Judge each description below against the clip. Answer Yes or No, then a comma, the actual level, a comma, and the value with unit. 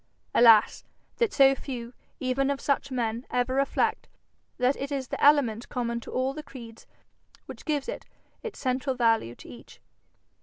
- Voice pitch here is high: Yes, very high, 255 Hz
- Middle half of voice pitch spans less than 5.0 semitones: Yes, average, 2.8 semitones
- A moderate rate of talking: Yes, average, 155 wpm